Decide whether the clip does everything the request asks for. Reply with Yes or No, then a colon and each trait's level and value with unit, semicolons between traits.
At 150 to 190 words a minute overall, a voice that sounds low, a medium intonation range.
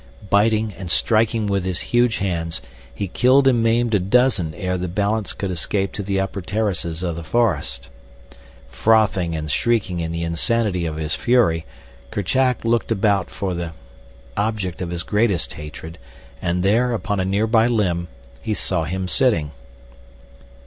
Yes: average, 160 wpm; low, 100 Hz; average, 4.6 semitones